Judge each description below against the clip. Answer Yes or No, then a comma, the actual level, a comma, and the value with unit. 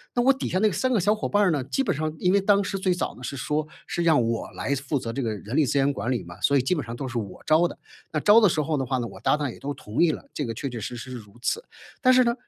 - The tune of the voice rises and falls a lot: Yes, wide, 7.2 semitones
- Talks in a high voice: No, medium, 150 Hz